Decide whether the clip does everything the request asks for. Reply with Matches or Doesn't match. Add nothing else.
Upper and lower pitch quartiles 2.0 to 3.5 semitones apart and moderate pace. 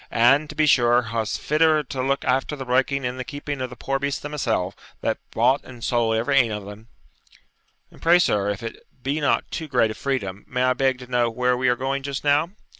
Doesn't match